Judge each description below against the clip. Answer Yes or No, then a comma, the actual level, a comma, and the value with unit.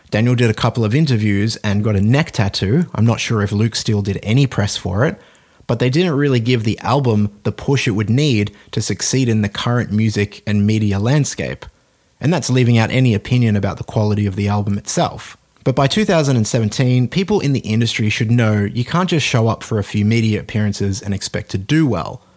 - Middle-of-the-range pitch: No, low, 110 Hz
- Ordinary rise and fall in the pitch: Yes, average, 3.3 semitones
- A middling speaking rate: No, fast, 215 wpm